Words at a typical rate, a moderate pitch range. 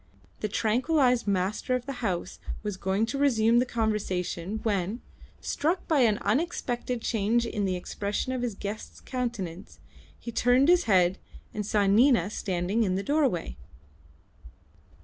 Yes: average, 145 wpm; average, 4.2 semitones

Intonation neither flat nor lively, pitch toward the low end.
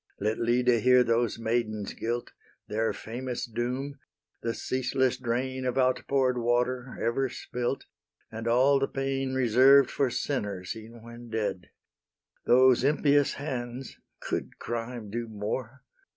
No: narrow, 2.1 semitones; low, 120 Hz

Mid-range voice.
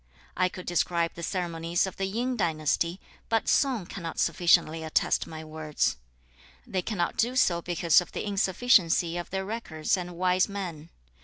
Yes: medium, 175 Hz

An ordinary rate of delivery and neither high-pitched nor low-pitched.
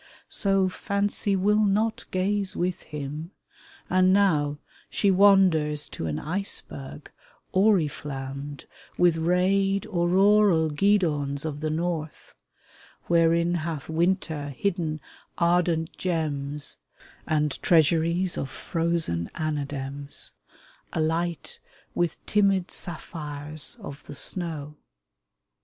No: slow, 95 wpm; medium, 165 Hz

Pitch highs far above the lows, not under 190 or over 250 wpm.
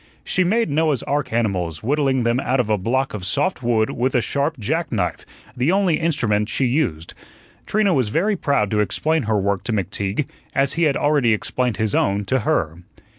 Yes: wide, 6.1 semitones; average, 195 wpm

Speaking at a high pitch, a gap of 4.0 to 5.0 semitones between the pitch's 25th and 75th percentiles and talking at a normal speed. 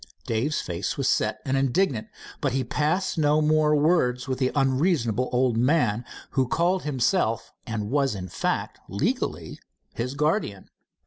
No: low, 135 Hz; average, 4.6 semitones; average, 145 wpm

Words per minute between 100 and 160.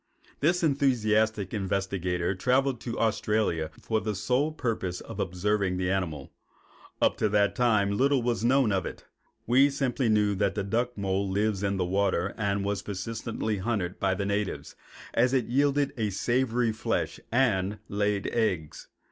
Yes: average, 155 wpm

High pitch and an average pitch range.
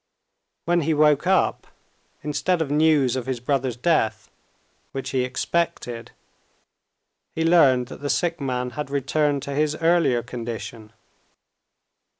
No: medium, 140 Hz; average, 4.1 semitones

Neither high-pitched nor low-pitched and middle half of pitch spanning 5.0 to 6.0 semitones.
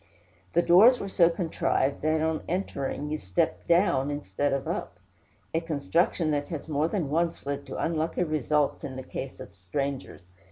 No: medium, 155 Hz; average, 3.3 semitones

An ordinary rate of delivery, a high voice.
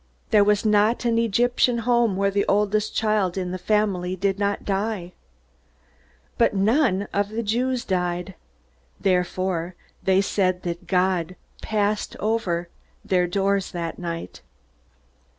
No: slow, 130 wpm; high, 200 Hz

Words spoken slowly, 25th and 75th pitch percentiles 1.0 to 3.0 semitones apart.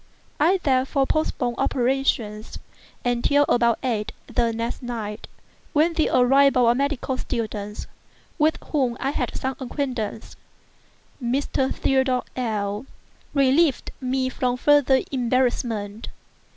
Yes: slow, 110 wpm; average, 2.7 semitones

